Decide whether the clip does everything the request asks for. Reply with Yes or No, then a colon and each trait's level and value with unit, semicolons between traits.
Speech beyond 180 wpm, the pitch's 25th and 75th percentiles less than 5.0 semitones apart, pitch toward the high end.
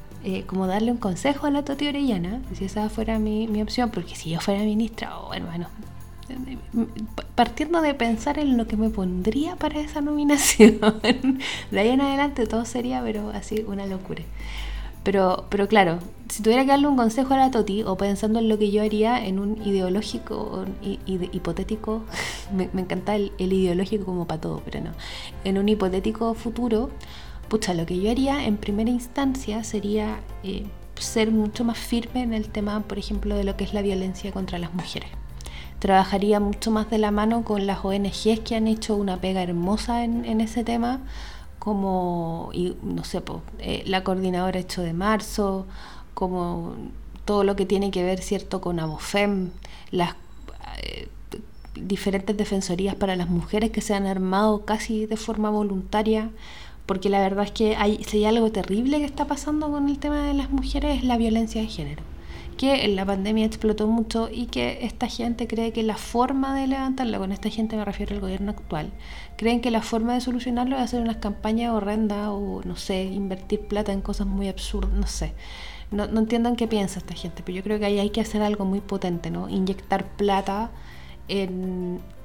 Yes: fast, 190 wpm; average, 2.9 semitones; high, 210 Hz